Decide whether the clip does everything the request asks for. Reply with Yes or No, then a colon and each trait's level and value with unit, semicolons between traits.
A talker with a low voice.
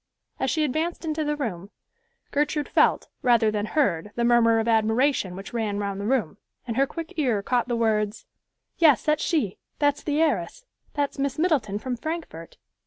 No: high, 245 Hz